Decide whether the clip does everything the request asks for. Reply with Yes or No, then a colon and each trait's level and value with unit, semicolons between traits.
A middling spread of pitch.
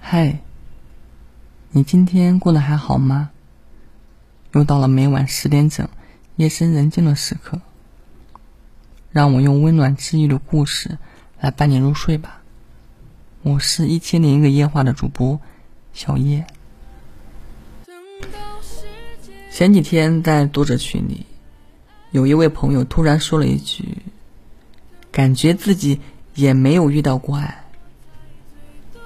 Yes: average, 3.2 semitones